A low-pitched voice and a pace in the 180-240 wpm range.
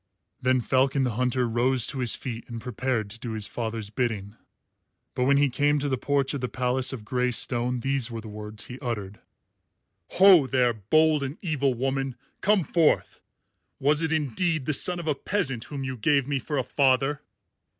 Yes: low, 130 Hz; average, 190 wpm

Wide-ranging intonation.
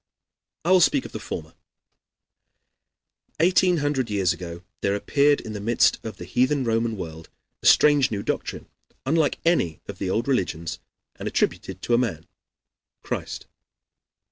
Yes: wide, 7.3 semitones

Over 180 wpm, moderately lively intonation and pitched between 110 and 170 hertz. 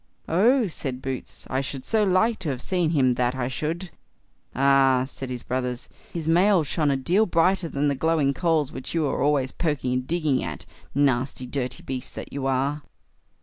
Yes: average, 190 wpm; average, 4.2 semitones; medium, 140 Hz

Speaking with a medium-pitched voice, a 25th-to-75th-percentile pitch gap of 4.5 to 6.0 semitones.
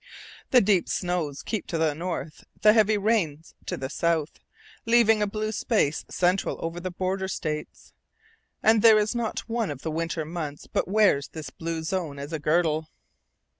Yes: medium, 175 Hz; average, 5.1 semitones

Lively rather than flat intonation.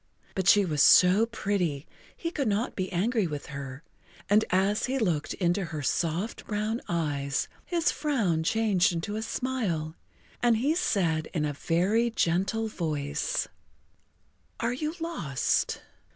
Yes: wide, 6.0 semitones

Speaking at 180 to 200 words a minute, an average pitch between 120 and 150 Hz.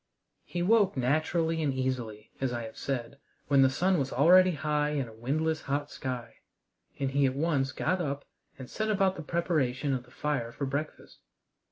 Yes: average, 185 wpm; medium, 140 Hz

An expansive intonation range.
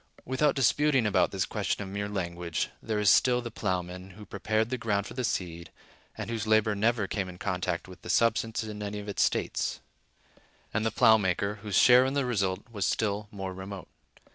No: average, 3.1 semitones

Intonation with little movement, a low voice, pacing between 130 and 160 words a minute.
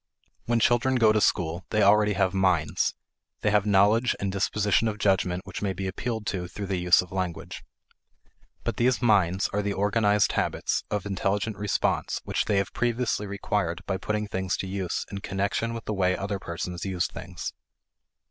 No: narrow, 2.1 semitones; low, 100 Hz; average, 180 wpm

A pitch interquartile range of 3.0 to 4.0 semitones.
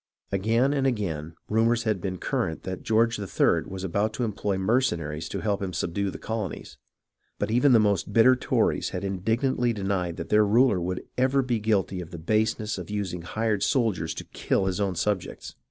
Yes: average, 3.7 semitones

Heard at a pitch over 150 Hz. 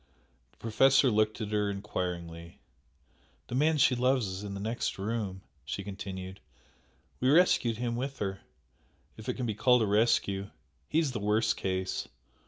No: low, 105 Hz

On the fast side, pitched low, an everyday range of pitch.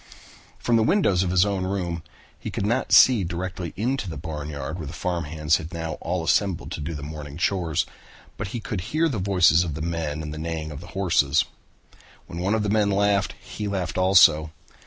Yes: fast, 210 wpm; very low, 85 Hz; average, 4.0 semitones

